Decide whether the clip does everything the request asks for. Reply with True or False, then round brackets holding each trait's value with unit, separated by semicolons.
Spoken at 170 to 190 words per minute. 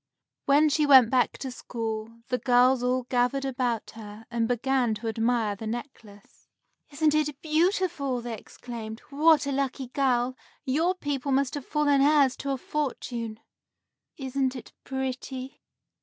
False (145 wpm)